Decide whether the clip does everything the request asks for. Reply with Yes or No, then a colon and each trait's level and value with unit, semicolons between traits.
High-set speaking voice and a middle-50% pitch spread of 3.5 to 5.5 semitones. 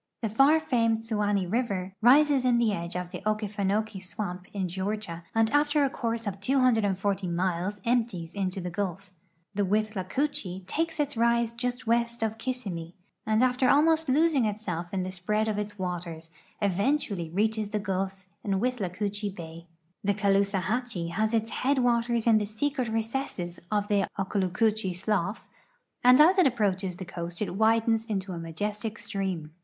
Yes: high, 210 Hz; average, 3.9 semitones